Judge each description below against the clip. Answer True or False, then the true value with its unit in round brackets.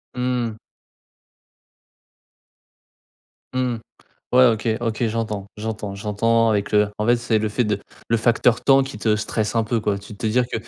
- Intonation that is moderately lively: False (2.1 semitones)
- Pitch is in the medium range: False (110 Hz)